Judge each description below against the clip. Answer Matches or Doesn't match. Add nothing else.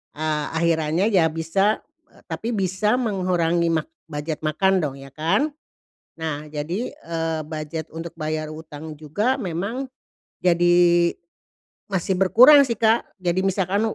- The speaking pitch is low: Doesn't match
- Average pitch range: Matches